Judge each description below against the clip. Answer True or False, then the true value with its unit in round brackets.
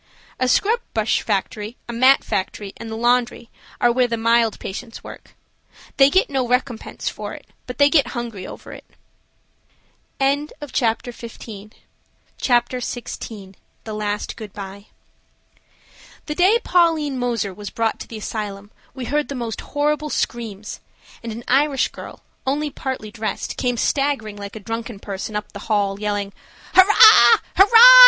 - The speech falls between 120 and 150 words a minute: True (145 wpm)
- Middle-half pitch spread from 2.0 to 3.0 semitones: False (4.2 semitones)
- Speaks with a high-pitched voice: True (235 Hz)